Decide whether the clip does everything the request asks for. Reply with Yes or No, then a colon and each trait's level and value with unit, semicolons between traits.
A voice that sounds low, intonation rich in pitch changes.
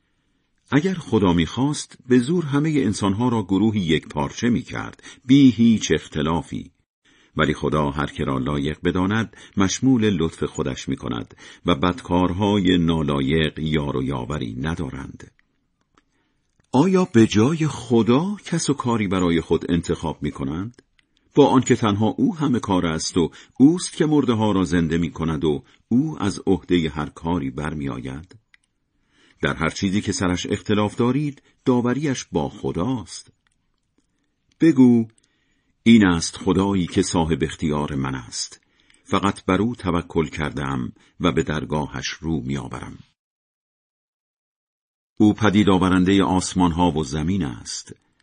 Yes: very low, 95 Hz; wide, 6.2 semitones